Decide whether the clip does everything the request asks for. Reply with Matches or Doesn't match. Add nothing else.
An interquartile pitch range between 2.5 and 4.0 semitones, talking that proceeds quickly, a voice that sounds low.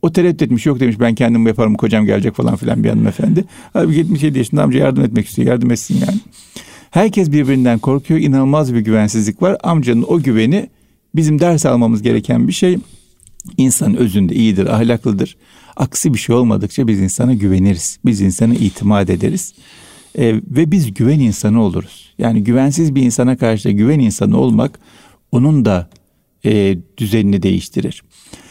Doesn't match